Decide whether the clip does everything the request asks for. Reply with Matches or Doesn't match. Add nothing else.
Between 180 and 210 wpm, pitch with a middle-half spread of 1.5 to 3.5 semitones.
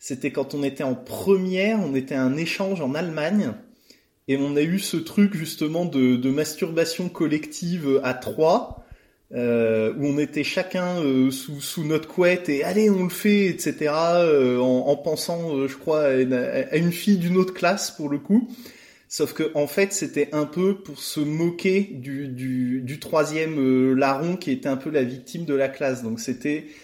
Doesn't match